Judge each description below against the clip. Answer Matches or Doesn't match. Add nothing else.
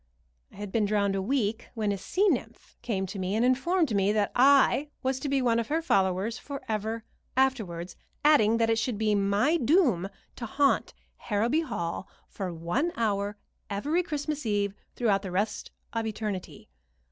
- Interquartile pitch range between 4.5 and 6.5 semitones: Matches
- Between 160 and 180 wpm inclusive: Matches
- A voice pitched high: Matches